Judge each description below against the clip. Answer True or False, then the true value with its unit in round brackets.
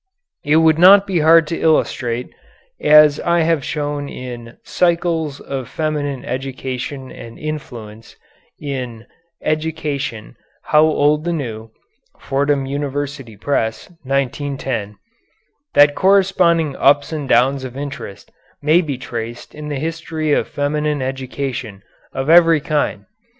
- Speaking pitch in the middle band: True (145 Hz)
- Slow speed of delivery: True (120 wpm)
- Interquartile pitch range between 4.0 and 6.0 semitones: False (3.1 semitones)